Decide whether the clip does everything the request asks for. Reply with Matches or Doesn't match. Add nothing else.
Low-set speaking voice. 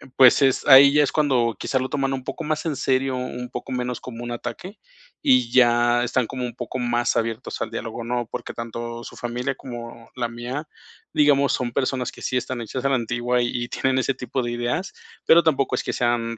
Matches